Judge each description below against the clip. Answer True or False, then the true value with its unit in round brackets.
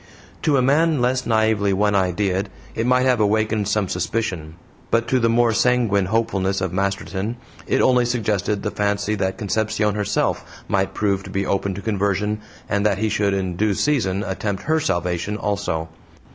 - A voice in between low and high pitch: False (105 Hz)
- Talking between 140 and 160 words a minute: False (175 wpm)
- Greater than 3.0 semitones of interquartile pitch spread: False (2.7 semitones)